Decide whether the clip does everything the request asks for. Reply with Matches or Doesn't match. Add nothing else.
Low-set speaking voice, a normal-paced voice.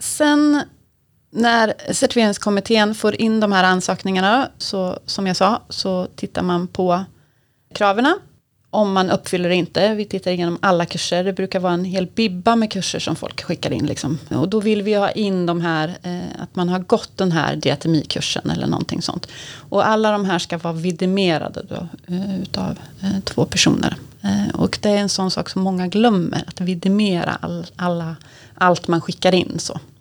Doesn't match